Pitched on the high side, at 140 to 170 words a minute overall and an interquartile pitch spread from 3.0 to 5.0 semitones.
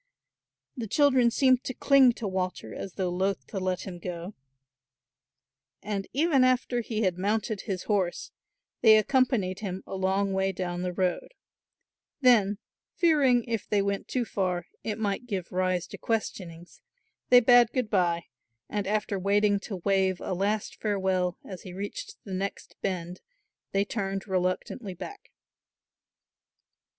Yes: high, 200 Hz; average, 145 wpm; average, 3.7 semitones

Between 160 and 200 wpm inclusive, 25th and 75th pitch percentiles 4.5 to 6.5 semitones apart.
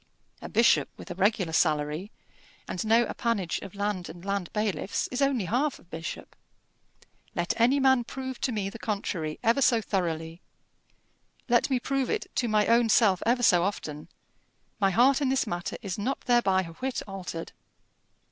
Yes: average, 170 wpm; wide, 5.6 semitones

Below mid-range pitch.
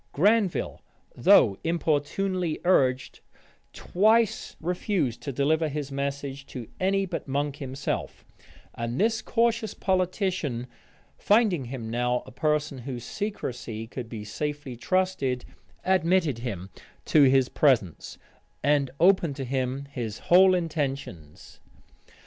No: medium, 145 Hz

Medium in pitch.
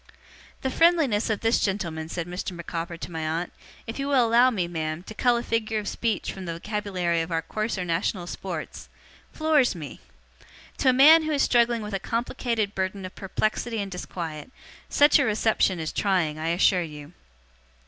No: high, 195 Hz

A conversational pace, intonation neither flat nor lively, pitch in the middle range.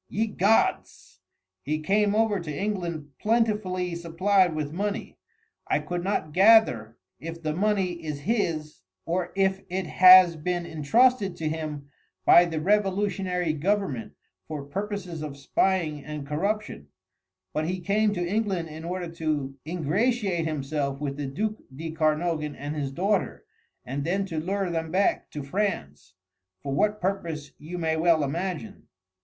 Yes: average, 145 wpm; average, 4.4 semitones; medium, 170 Hz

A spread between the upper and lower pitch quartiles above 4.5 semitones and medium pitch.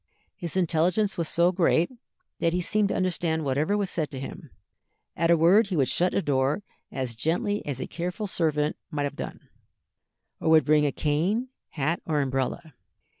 No: average, 3.6 semitones; medium, 165 Hz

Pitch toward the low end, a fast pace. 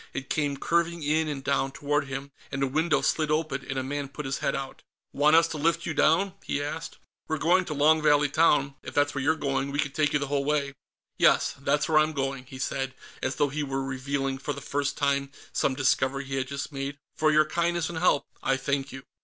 No: medium, 145 Hz; fast, 240 wpm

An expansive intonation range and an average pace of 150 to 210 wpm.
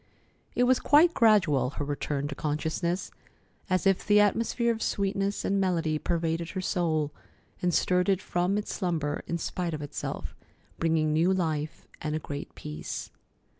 No: average, 4.2 semitones; average, 160 wpm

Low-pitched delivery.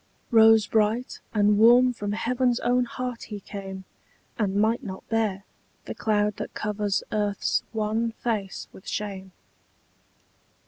No: high, 215 Hz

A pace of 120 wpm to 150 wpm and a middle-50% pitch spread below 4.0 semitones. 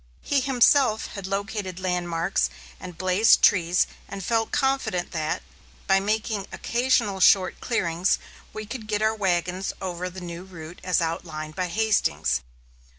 Yes: average, 140 wpm; average, 3.6 semitones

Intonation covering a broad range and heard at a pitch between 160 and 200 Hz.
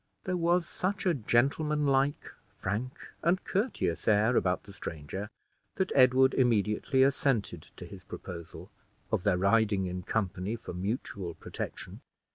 No: wide, 6.6 semitones; low, 115 Hz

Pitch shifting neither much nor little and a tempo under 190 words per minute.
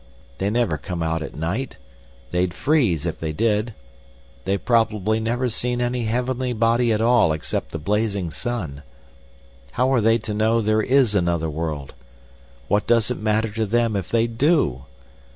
No: wide, 5.7 semitones; average, 160 wpm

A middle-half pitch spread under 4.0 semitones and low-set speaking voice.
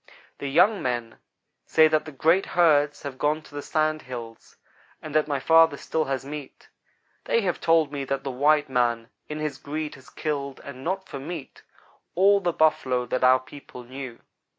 No: average, 3.1 semitones; medium, 145 Hz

